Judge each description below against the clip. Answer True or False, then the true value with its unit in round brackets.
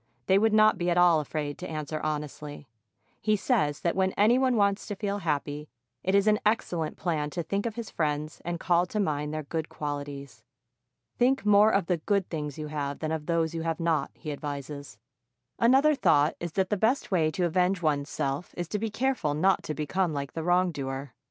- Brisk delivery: True (210 wpm)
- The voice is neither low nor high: True (170 Hz)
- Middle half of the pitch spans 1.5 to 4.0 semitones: False (5.0 semitones)